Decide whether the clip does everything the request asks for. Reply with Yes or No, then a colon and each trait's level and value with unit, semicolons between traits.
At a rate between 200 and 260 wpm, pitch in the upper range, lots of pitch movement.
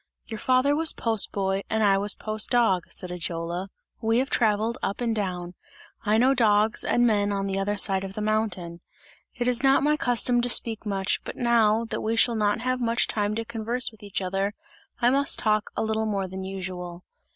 No: fast, 205 wpm; high, 215 Hz; average, 3.3 semitones